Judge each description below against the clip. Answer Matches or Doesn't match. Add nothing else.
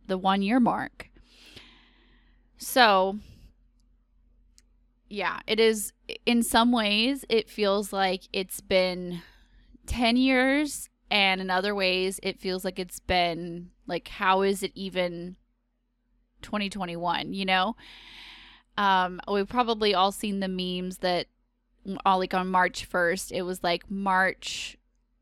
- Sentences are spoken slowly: Matches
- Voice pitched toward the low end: Doesn't match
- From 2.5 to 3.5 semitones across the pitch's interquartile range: Matches